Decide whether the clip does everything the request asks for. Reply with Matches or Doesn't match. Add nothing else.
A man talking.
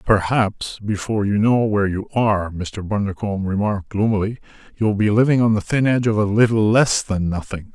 Matches